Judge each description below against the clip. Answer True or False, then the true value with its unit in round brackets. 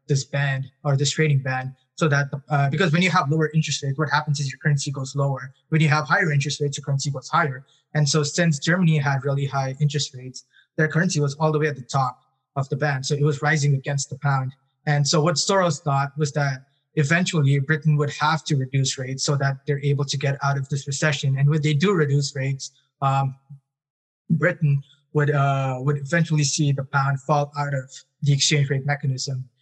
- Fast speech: True (220 wpm)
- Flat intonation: True (1.7 semitones)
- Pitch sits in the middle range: True (145 Hz)